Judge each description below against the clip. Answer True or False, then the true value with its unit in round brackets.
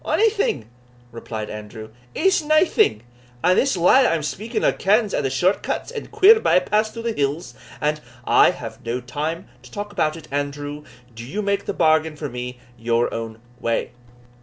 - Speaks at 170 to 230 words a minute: True (185 wpm)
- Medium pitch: True (155 Hz)